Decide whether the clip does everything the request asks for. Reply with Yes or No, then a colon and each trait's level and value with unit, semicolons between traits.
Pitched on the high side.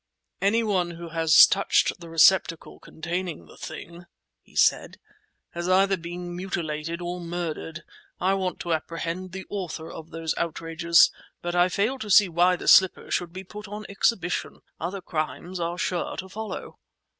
No: medium, 175 Hz